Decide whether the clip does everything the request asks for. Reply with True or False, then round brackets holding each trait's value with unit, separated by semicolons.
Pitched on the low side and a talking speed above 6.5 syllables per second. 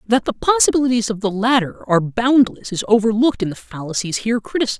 False (215 Hz; 6.7 syllables/s)